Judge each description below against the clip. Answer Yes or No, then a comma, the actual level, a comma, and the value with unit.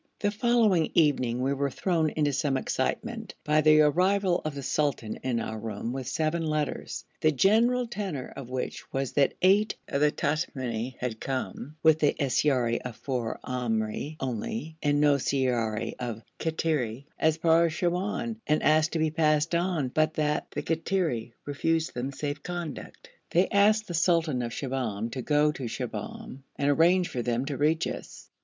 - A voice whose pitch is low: No, medium, 150 Hz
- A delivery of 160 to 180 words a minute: Yes, average, 170 wpm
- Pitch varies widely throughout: No, average, 4.4 semitones